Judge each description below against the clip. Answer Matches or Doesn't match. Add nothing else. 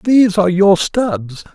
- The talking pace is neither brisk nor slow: Matches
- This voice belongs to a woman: Doesn't match